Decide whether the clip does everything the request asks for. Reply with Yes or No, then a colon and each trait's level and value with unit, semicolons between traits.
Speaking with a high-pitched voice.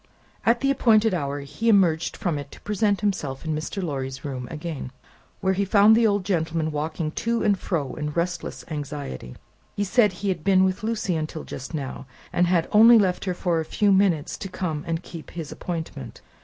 No: medium, 175 Hz